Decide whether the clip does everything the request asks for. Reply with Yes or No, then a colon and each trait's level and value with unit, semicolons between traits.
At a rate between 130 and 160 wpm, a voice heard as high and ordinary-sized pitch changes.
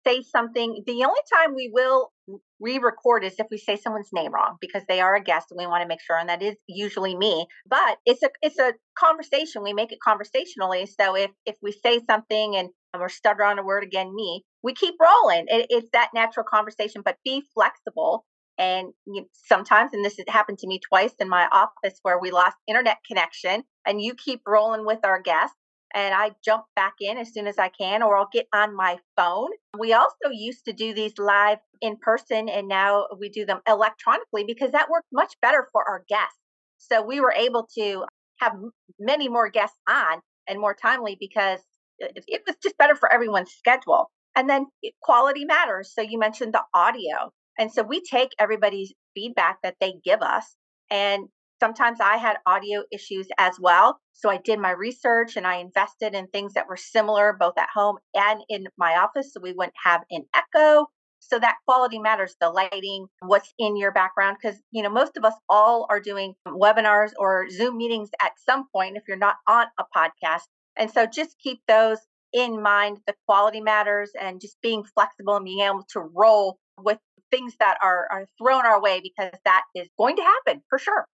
No: average, 200 wpm; high, 215 Hz; average, 3.3 semitones